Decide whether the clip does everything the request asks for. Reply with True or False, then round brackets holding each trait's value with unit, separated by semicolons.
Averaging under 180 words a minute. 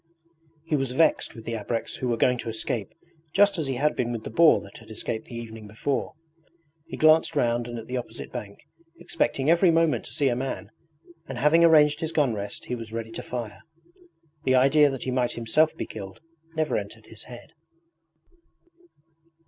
False (195 wpm)